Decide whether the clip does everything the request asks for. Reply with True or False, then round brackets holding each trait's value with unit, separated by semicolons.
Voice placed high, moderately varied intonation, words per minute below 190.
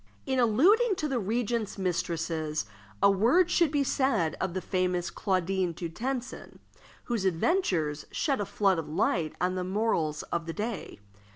False (195 Hz; 6.7 semitones; 160 wpm)